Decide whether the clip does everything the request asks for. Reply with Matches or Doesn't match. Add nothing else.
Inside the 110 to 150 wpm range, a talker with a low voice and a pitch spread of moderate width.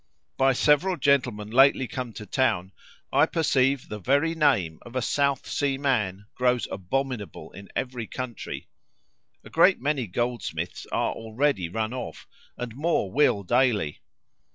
Matches